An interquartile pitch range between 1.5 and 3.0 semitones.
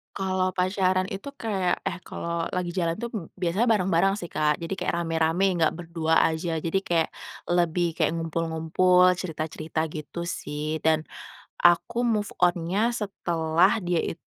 Yes: narrow, 2.5 semitones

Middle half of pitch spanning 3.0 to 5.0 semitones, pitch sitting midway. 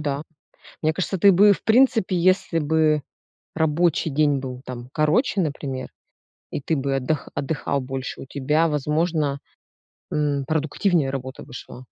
Yes: average, 3.3 semitones; medium, 150 Hz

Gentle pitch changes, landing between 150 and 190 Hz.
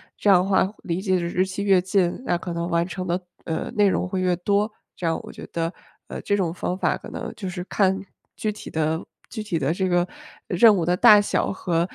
Yes: narrow, 2.3 semitones; medium, 185 Hz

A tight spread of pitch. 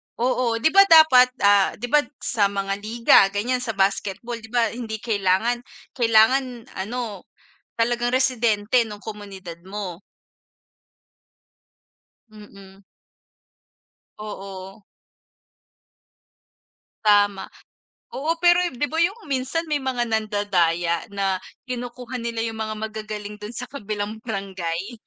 No: average, 3.5 semitones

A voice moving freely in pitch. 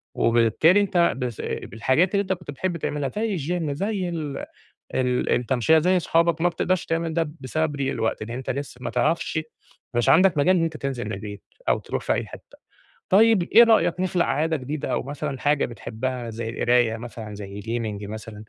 Yes: wide, 6.2 semitones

